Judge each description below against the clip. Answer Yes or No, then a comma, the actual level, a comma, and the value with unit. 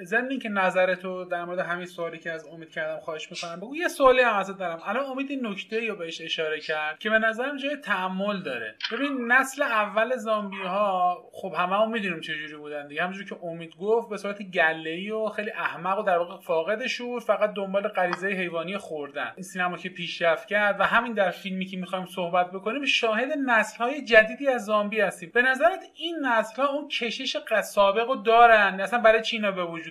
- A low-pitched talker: No, high, 200 Hz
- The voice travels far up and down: No, average, 4.5 semitones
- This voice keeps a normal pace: No, fast, 200 wpm